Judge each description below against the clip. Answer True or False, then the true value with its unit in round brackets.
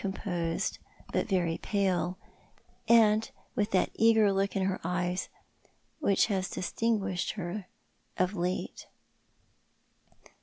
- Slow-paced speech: True (105 wpm)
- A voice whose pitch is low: False (190 Hz)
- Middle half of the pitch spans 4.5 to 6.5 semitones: False (2.6 semitones)